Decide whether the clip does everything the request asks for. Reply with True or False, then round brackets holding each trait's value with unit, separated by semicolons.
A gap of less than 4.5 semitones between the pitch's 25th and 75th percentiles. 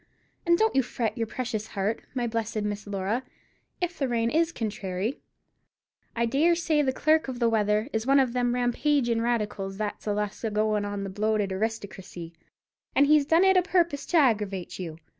False (4.8 semitones)